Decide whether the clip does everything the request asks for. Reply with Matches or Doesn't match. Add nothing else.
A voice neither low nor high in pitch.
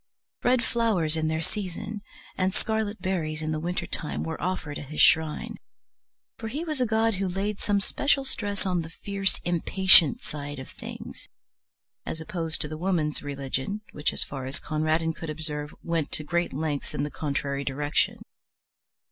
Matches